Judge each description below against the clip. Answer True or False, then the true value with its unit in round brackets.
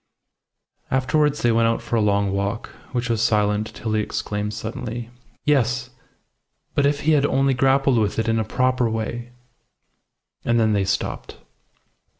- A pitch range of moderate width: True (3.1 semitones)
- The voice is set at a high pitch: False (115 Hz)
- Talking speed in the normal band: True (160 wpm)